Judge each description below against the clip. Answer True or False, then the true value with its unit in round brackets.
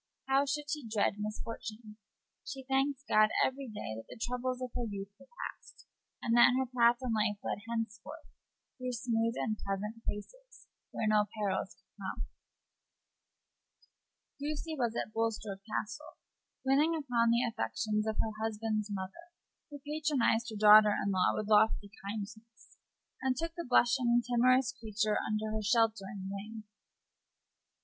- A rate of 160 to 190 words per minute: False (145 wpm)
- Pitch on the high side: True (225 Hz)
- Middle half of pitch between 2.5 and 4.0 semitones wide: True (3.3 semitones)